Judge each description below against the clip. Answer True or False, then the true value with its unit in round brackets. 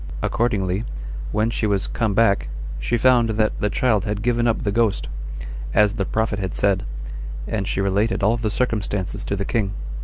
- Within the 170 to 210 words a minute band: True (180 wpm)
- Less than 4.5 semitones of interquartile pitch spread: True (2.5 semitones)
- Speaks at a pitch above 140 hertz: False (105 Hz)